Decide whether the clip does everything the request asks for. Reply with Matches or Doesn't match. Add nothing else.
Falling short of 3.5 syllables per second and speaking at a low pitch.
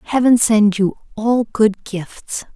Doesn't match